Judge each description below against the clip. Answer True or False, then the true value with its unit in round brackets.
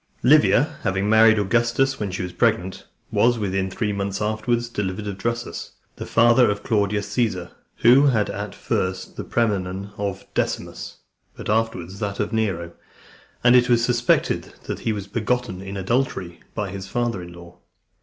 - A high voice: False (105 Hz)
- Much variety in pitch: False (3.5 semitones)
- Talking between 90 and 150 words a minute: False (165 wpm)